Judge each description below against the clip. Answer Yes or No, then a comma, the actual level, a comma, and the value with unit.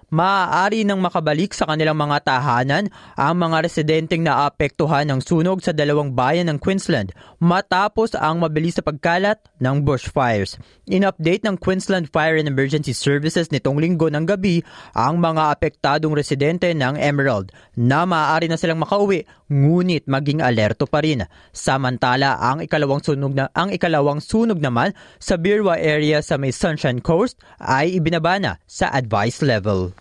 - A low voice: No, medium, 155 Hz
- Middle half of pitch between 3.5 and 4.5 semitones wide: Yes, average, 4.1 semitones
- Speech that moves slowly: No, average, 150 wpm